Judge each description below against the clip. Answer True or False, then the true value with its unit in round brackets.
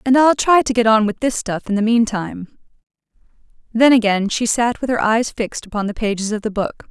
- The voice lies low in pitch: False (225 Hz)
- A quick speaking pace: True (225 wpm)